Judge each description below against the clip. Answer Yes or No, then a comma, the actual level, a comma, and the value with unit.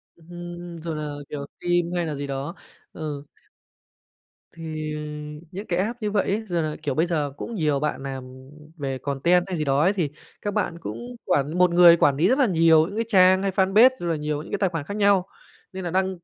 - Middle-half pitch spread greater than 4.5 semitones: No, average, 4.0 semitones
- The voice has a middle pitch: Yes, medium, 170 Hz